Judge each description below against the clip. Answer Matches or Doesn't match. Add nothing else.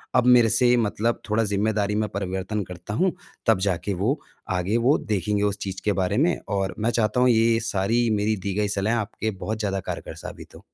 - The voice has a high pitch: Doesn't match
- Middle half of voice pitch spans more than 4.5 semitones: Doesn't match